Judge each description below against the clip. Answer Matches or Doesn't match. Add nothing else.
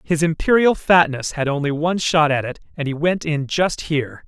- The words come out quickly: Matches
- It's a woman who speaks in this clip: Doesn't match